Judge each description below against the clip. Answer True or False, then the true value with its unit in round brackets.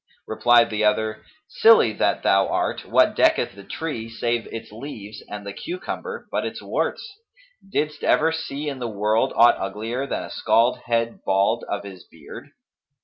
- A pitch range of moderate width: False (5.8 semitones)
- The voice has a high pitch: False (115 Hz)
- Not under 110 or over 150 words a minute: False (165 wpm)